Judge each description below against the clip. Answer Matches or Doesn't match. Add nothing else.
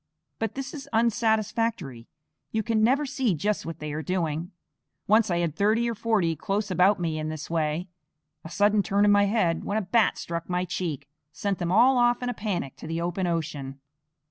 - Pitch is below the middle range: Doesn't match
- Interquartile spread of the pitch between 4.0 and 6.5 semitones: Matches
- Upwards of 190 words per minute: Matches